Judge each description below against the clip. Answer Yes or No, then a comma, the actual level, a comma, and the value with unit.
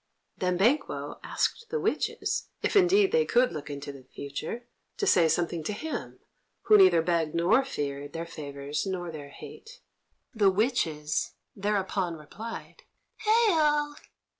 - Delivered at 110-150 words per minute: Yes, average, 140 wpm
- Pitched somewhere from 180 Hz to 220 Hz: Yes, high, 190 Hz